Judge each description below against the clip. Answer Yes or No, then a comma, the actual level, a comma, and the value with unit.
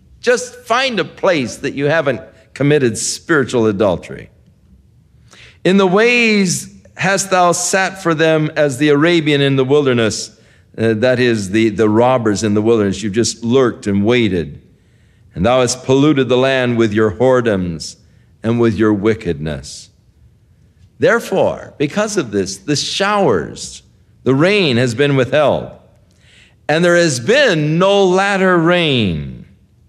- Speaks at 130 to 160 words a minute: Yes, average, 140 wpm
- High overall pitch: No, low, 125 Hz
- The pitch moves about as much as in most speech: No, wide, 6.9 semitones